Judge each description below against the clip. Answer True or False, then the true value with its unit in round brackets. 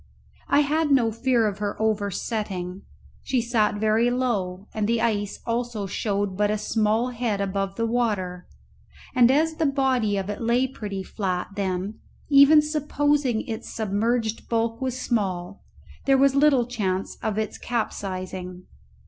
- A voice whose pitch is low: False (220 Hz)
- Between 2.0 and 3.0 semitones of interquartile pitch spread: False (3.9 semitones)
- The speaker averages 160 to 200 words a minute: False (150 wpm)